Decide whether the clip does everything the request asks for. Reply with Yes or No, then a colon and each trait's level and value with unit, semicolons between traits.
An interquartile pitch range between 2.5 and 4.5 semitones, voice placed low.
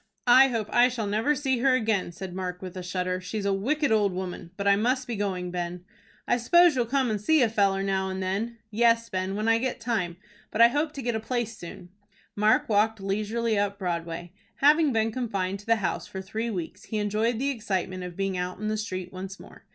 No: average, 3.8 semitones; high, 210 Hz